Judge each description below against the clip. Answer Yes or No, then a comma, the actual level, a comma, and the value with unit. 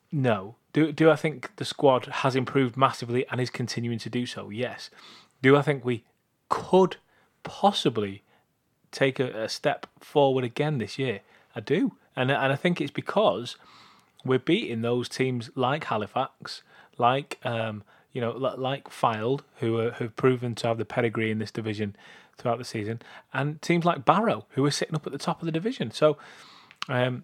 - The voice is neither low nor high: No, low, 130 Hz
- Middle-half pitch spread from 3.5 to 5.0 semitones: Yes, average, 4.0 semitones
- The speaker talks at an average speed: Yes, average, 175 wpm